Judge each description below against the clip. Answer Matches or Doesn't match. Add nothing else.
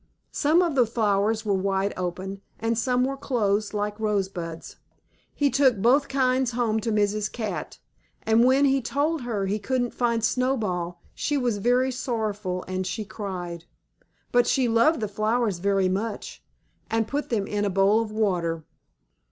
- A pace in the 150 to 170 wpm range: Matches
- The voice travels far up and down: Doesn't match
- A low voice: Doesn't match